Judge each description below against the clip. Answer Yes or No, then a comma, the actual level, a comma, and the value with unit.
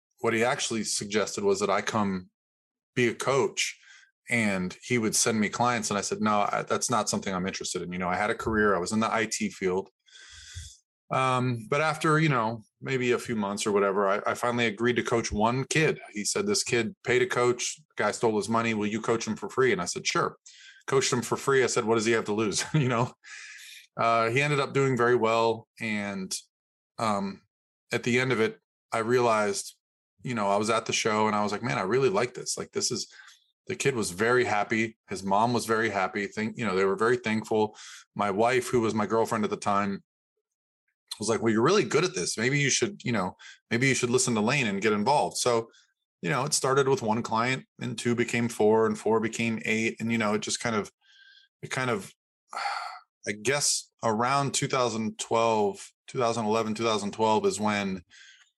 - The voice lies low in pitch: Yes, low, 115 Hz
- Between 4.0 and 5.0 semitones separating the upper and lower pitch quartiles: No, average, 3.2 semitones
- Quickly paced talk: Yes, fast, 215 wpm